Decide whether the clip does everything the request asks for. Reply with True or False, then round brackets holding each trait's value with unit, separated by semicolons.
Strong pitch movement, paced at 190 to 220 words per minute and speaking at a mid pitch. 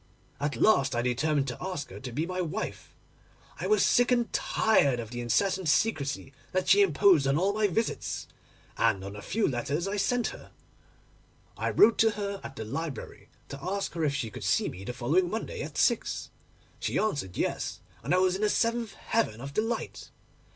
True (7.3 semitones; 195 wpm; 170 Hz)